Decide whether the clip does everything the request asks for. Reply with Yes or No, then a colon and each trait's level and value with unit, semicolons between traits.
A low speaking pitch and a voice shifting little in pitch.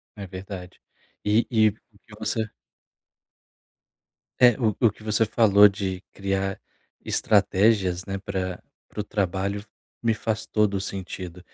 Yes: low, 100 Hz; narrow, 2.2 semitones